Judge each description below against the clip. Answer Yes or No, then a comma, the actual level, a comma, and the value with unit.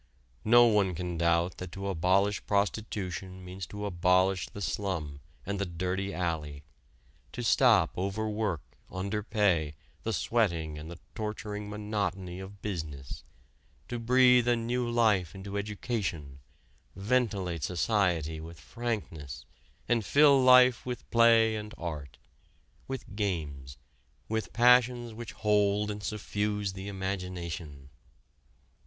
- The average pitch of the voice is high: No, low, 100 Hz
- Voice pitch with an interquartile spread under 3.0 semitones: No, average, 4.1 semitones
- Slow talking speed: Yes, slow, 120 wpm